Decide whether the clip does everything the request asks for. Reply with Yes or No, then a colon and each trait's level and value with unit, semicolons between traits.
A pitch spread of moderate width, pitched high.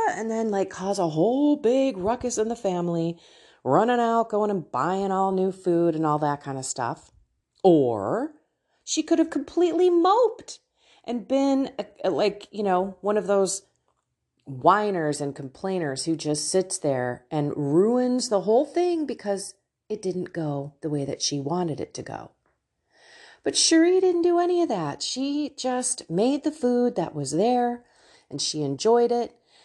No: wide, 7.4 semitones; high, 200 Hz